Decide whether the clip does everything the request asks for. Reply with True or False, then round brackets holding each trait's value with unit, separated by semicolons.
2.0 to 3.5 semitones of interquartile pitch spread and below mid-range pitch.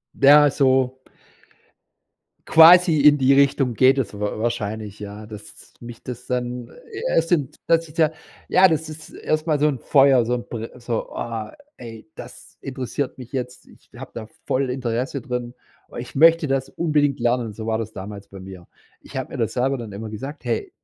False (4.3 semitones; 125 Hz)